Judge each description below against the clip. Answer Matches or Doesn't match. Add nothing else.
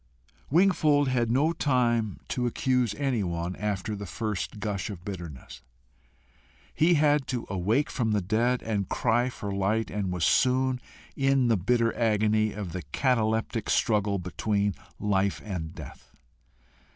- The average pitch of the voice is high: Doesn't match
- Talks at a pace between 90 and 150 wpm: Matches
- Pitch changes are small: Doesn't match